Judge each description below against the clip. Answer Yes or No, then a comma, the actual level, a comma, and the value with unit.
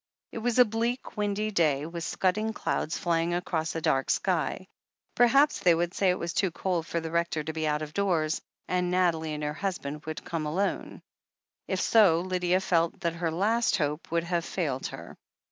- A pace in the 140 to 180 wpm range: No, average, 195 wpm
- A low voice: No, medium, 170 Hz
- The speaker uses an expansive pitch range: No, average, 3.3 semitones